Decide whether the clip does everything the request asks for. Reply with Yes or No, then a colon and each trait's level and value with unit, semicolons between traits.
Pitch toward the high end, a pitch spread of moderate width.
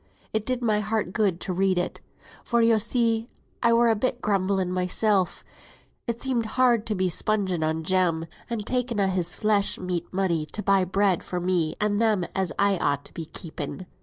Yes: high, 200 Hz; average, 3.6 semitones